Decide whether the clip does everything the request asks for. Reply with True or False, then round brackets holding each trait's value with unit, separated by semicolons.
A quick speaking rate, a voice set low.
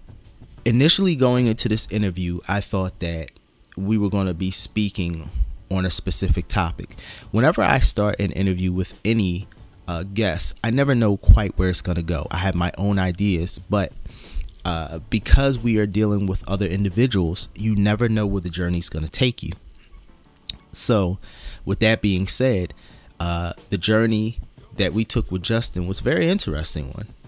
False (175 wpm; 95 Hz)